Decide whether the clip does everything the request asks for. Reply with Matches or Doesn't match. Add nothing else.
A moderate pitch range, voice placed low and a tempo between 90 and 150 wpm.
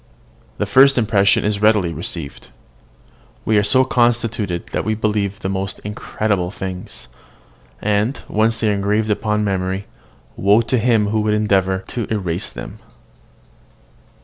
Doesn't match